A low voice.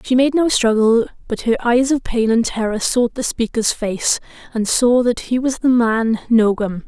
No: high, 235 Hz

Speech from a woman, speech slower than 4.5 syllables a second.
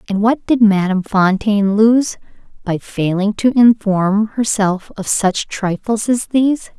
Yes: female; 4.1 syllables/s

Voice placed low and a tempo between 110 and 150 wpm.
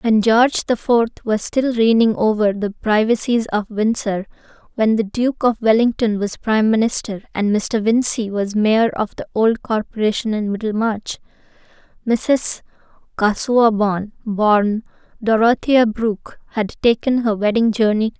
No: high, 220 Hz; average, 140 wpm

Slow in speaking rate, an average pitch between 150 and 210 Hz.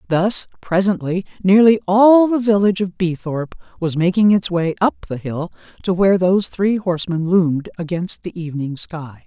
No: average, 160 wpm; medium, 185 Hz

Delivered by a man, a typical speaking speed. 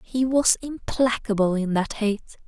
No: female; average, 145 wpm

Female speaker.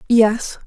Yes: female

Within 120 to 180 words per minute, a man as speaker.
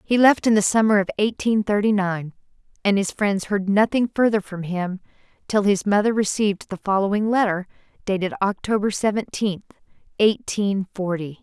No: average, 150 wpm; female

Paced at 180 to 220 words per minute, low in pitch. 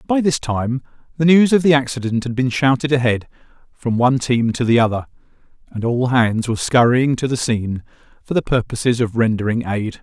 Yes: average, 190 wpm; low, 125 Hz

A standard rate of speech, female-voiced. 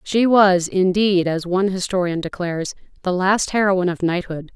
Yes: average, 160 wpm; female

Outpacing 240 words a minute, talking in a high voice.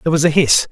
No: fast, 335 wpm; medium, 155 Hz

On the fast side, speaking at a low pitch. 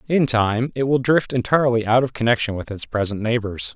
Yes: fast, 210 wpm; low, 120 Hz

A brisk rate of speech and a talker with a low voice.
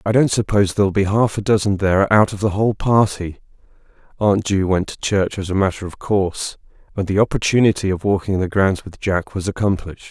Yes: fast, 215 wpm; low, 100 Hz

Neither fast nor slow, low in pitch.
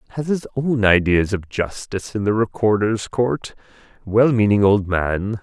Yes: average, 145 wpm; low, 105 Hz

